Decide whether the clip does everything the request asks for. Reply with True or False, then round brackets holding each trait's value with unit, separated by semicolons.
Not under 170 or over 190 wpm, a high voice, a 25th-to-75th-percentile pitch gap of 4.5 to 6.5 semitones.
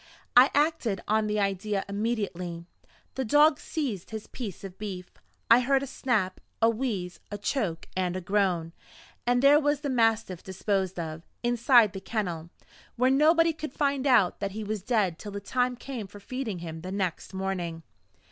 True (175 wpm; 210 Hz; 5.2 semitones)